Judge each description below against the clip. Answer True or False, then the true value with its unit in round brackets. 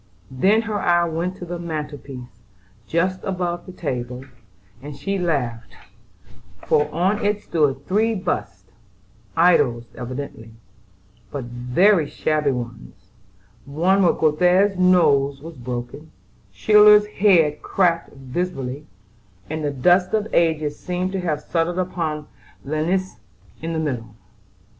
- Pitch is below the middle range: False (160 Hz)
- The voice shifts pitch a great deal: False (5.0 semitones)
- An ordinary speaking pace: False (120 wpm)